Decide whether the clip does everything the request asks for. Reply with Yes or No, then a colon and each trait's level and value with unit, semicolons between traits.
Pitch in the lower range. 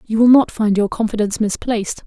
No: high, 220 Hz